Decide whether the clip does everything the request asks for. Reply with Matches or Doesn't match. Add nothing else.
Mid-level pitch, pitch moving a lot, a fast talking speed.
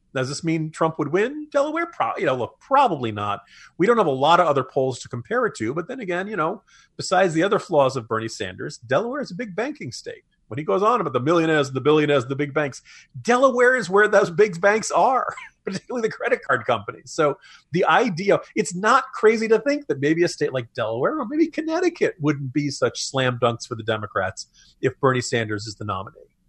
Matches